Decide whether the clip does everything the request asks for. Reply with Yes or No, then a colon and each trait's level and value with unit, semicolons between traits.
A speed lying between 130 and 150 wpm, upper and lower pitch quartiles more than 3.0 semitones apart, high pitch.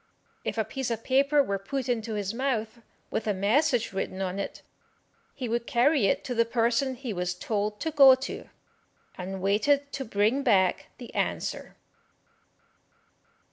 No: average, 160 wpm; average, 4.7 semitones; high, 230 Hz